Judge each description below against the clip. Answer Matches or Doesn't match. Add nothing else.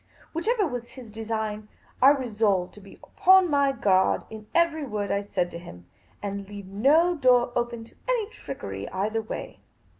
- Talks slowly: Doesn't match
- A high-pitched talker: Matches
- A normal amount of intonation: Doesn't match